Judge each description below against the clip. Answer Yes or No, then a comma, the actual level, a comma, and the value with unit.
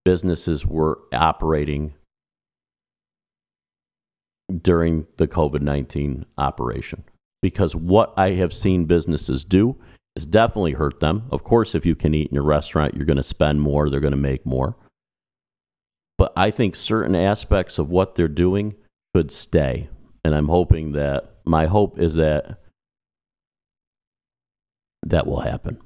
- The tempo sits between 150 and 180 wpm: No, slow, 135 wpm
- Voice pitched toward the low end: Yes, very low, 80 Hz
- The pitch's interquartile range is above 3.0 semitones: Yes, average, 4.3 semitones